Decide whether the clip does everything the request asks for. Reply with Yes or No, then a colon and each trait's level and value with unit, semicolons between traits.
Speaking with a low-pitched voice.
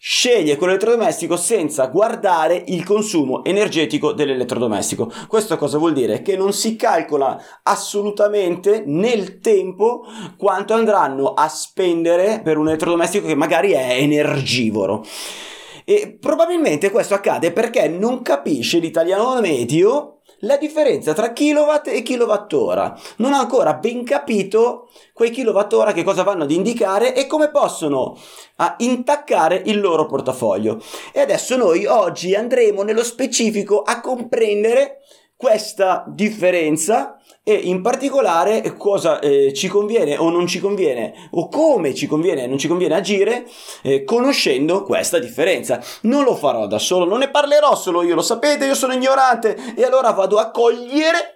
No: high, 210 Hz